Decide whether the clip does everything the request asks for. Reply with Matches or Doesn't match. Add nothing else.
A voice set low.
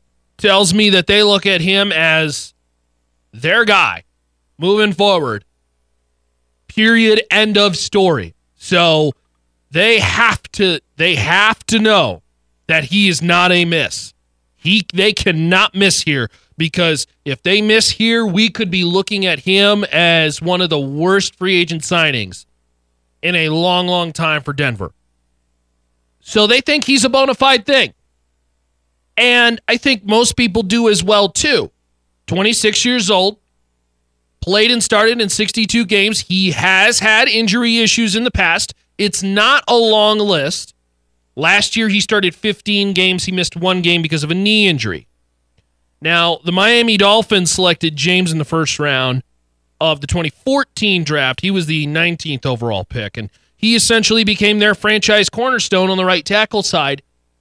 Doesn't match